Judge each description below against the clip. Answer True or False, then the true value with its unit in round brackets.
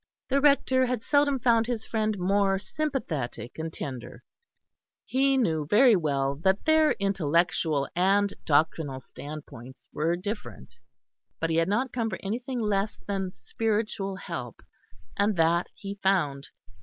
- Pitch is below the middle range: False (195 Hz)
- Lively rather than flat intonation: True (6.3 semitones)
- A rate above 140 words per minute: False (135 wpm)